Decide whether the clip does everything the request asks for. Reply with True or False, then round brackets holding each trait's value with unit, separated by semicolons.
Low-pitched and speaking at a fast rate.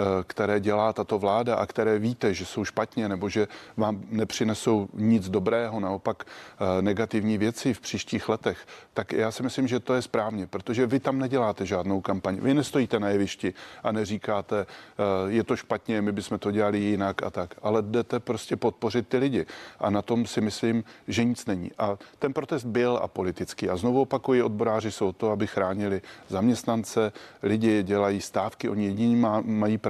True (110 Hz; 175 wpm)